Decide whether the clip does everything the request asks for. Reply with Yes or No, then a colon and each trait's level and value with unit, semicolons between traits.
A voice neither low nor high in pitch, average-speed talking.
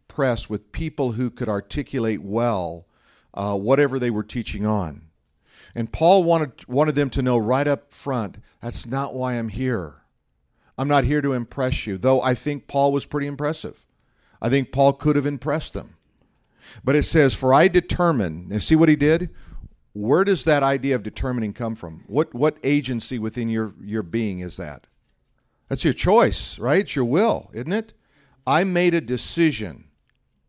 No: low, 130 Hz; average, 175 wpm